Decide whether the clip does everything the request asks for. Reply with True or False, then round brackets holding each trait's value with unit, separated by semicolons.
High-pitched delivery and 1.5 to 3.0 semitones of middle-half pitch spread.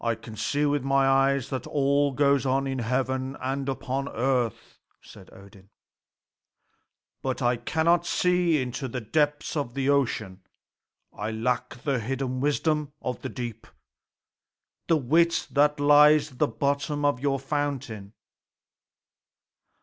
False (135 Hz; 2.7 semitones)